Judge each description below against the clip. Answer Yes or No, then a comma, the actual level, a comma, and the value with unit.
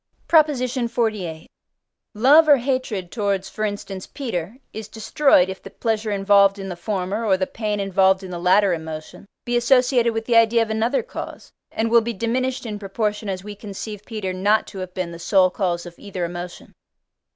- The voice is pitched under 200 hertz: No, high, 210 Hz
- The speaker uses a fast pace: No, average, 185 wpm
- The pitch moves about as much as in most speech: Yes, average, 3.5 semitones